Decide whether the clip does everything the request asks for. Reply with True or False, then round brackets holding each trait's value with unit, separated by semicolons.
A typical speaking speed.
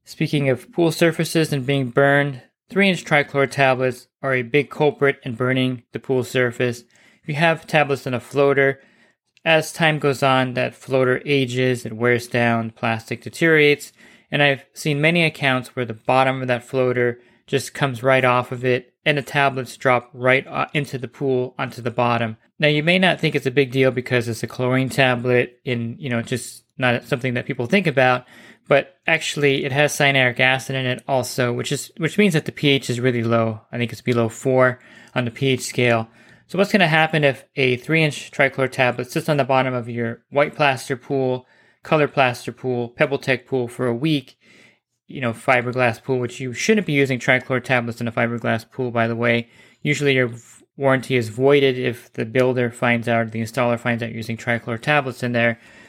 True (195 wpm)